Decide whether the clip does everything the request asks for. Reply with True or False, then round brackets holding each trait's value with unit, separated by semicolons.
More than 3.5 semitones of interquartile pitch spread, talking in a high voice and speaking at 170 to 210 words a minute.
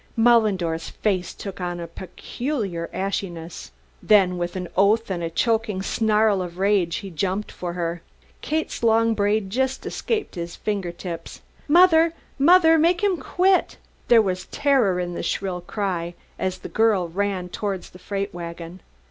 False (4.3 semitones; 195 Hz; 155 wpm)